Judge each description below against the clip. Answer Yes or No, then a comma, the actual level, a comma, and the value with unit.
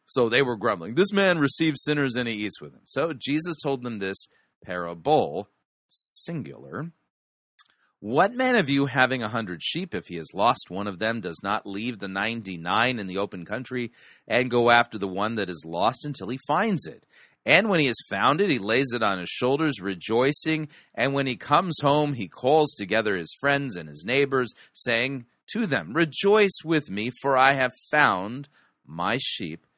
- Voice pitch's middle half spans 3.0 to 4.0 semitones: No, wide, 5.6 semitones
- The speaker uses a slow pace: No, average, 190 wpm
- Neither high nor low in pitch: No, low, 130 Hz